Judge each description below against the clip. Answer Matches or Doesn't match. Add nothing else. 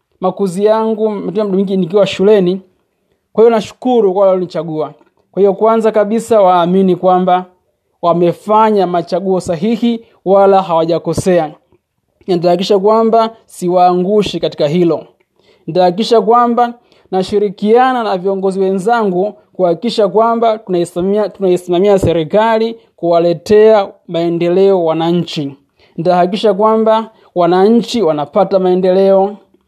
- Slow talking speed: Matches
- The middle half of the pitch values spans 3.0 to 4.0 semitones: Matches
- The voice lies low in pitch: Doesn't match